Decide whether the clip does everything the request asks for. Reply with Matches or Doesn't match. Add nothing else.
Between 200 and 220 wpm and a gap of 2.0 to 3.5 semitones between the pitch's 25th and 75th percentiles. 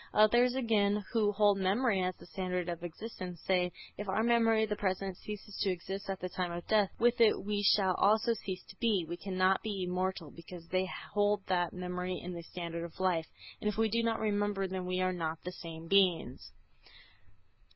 Matches